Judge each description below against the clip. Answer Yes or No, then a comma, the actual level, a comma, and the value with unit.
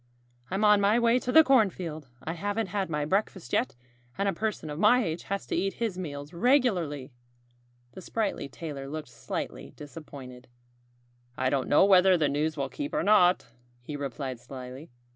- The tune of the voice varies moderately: No, wide, 6.1 semitones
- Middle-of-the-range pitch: Yes, medium, 170 Hz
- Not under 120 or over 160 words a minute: No, average, 175 wpm